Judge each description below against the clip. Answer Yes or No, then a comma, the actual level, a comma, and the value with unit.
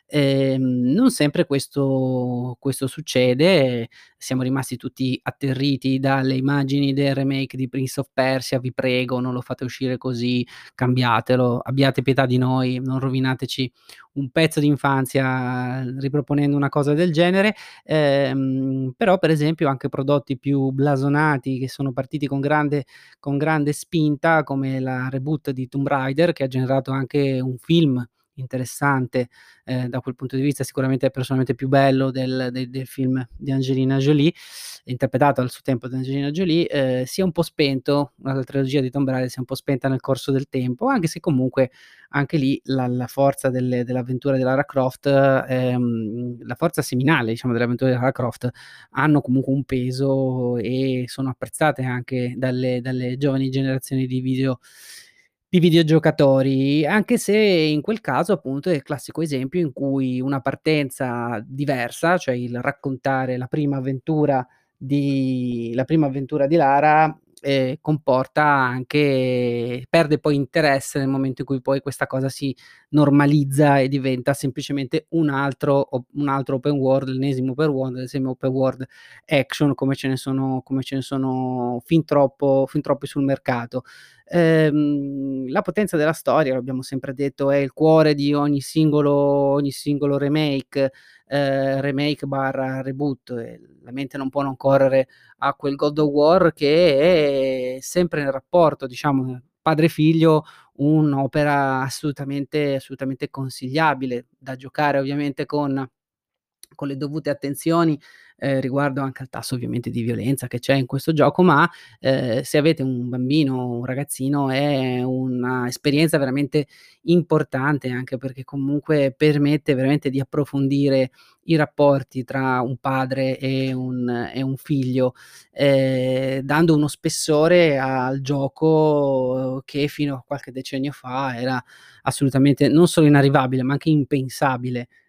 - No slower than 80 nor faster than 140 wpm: No, average, 150 wpm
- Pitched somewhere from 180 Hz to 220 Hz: No, low, 135 Hz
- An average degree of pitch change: No, narrow, 1.9 semitones